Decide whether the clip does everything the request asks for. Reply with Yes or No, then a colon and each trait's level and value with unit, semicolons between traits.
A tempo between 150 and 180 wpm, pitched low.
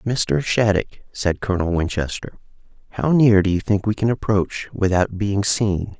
Yes: average, 160 wpm; low, 100 Hz